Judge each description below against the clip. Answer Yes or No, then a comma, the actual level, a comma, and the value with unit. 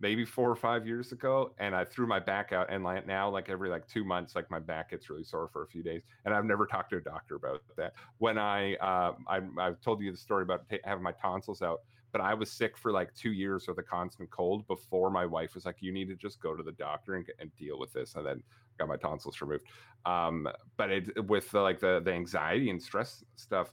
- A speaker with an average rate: No, fast, 260 wpm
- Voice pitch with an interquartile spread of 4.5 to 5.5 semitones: No, average, 3.7 semitones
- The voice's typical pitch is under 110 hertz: Yes, low, 100 Hz